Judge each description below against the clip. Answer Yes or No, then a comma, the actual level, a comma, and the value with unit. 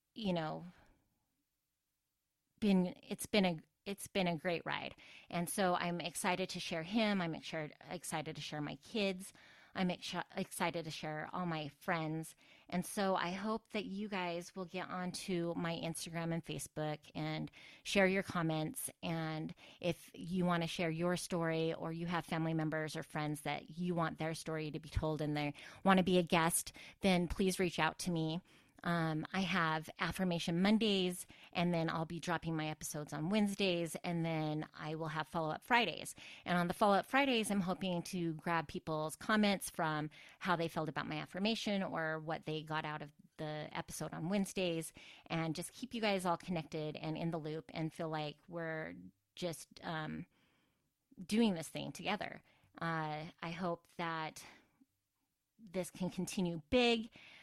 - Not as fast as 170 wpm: No, average, 175 wpm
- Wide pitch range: No, average, 2.9 semitones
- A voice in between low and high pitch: Yes, medium, 170 Hz